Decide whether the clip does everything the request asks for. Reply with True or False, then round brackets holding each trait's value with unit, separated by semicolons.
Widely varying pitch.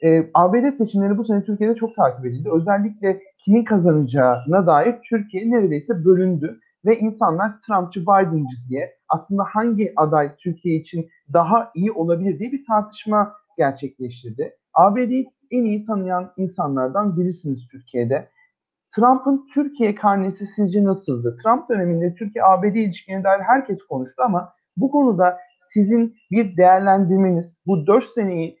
False (4.6 semitones)